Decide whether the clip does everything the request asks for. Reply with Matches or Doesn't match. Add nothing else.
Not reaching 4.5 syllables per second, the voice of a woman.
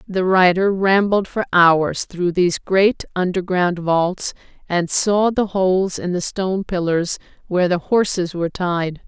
Matches